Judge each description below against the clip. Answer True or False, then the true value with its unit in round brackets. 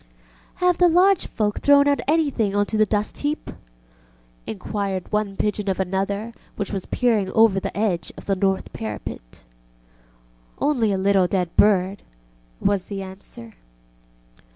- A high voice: True (200 Hz)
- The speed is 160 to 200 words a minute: False (145 wpm)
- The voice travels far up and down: False (2.9 semitones)